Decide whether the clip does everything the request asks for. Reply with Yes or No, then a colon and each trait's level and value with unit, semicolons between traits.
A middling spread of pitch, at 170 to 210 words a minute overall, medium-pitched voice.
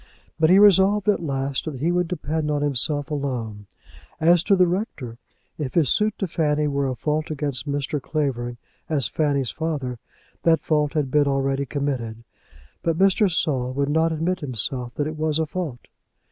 Yes: average, 3.1 semitones; average, 180 wpm; medium, 150 Hz